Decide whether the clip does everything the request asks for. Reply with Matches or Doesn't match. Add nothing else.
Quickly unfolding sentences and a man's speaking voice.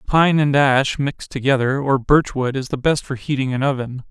Matches